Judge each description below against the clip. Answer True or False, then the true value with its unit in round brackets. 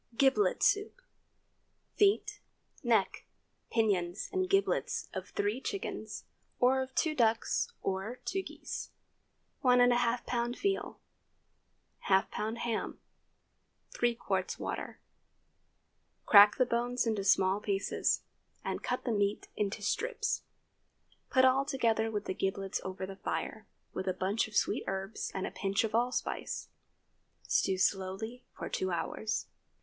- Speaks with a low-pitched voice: False (225 Hz)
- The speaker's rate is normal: False (125 wpm)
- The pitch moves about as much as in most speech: True (4.4 semitones)